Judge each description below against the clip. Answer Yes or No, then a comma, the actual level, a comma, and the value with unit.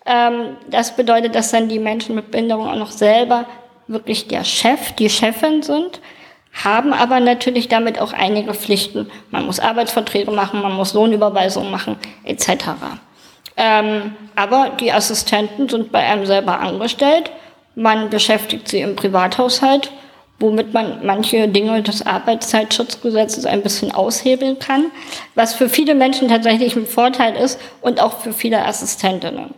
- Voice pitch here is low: No, high, 230 Hz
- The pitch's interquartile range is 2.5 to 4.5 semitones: Yes, average, 2.8 semitones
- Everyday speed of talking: Yes, average, 140 wpm